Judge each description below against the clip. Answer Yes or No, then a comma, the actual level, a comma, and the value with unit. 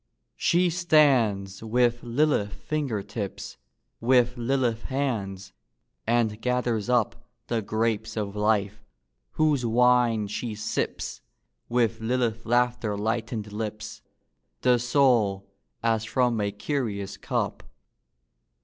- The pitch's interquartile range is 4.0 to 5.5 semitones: No, average, 2.8 semitones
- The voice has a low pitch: Yes, low, 115 Hz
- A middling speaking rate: No, slow, 105 wpm